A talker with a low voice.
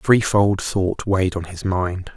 Yes: very low, 95 Hz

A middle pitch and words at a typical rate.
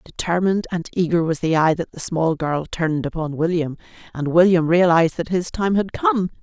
Yes: medium, 170 Hz; average, 195 wpm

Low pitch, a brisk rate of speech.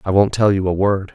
Yes: low, 100 Hz; fast, 315 wpm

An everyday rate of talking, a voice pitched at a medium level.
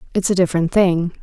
Yes: average, 195 wpm; medium, 180 Hz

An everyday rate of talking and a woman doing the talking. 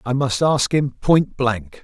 No: average, 195 wpm; male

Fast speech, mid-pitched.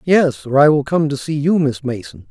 Yes: fast, 260 wpm; medium, 145 Hz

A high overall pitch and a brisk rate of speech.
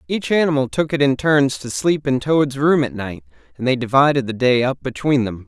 No: low, 135 Hz; fast, 230 wpm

